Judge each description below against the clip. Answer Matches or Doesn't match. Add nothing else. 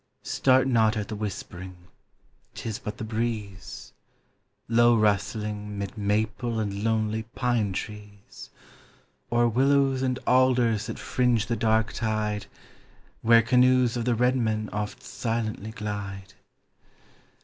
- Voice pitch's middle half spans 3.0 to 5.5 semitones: Doesn't match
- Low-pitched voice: Matches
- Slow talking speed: Matches